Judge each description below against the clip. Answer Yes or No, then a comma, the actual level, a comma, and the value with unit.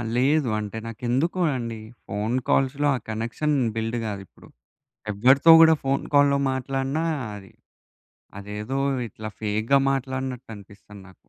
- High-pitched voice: No, low, 125 Hz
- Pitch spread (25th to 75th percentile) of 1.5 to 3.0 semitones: No, average, 4.2 semitones